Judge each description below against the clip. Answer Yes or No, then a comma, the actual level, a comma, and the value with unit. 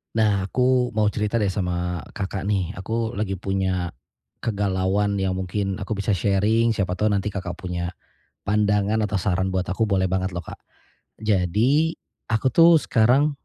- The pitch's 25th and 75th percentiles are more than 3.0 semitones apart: No, average, 2.7 semitones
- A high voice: No, low, 100 Hz